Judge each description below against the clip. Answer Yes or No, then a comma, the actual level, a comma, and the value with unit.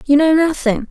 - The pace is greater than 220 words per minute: No, average, 200 wpm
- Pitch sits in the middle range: No, very high, 290 Hz